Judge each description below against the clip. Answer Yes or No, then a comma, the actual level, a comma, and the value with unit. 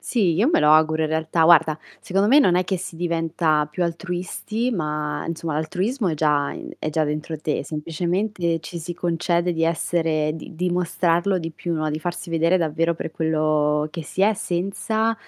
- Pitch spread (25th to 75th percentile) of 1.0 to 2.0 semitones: No, narrow, 2.5 semitones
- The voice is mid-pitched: Yes, medium, 165 Hz